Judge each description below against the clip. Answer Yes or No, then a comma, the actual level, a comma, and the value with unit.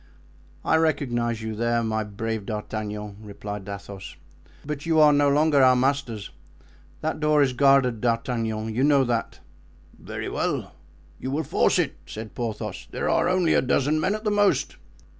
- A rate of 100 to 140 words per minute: No, average, 160 wpm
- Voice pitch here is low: Yes, low, 125 Hz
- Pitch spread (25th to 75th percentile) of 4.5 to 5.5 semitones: Yes, average, 5.1 semitones